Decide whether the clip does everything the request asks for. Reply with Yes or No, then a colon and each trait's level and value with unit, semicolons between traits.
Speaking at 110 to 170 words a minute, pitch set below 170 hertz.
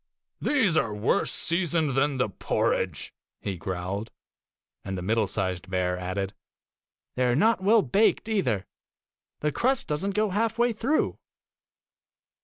Yes: average, 140 wpm; low, 135 Hz